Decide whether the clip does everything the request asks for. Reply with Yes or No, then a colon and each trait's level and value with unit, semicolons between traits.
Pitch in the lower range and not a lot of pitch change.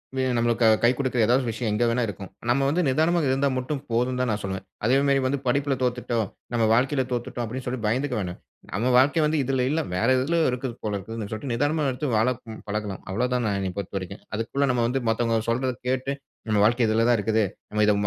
No: low, 120 Hz; average, 3.2 semitones